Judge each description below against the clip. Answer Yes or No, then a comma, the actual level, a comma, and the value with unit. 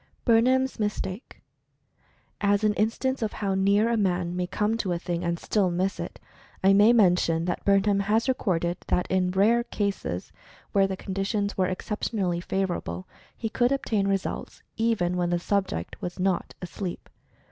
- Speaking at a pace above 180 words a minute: No, average, 160 wpm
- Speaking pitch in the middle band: No, high, 195 Hz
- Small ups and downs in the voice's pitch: No, average, 3.0 semitones